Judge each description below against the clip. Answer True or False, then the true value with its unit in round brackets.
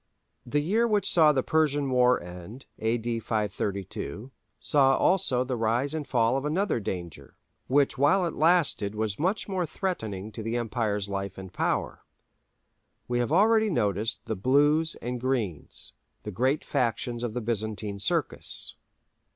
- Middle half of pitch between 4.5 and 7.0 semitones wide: True (5.6 semitones)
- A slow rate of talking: False (150 wpm)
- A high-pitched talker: False (120 Hz)